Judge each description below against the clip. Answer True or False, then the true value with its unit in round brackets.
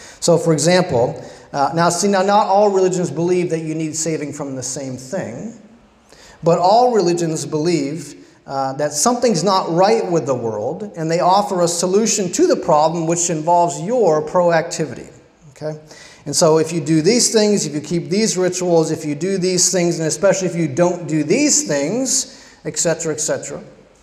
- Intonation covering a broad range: False (3.2 semitones)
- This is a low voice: False (170 Hz)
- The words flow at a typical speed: True (180 wpm)